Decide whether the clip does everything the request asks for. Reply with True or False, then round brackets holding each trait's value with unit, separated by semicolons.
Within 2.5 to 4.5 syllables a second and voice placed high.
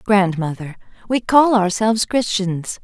True (4.2 syllables/s; 200 Hz)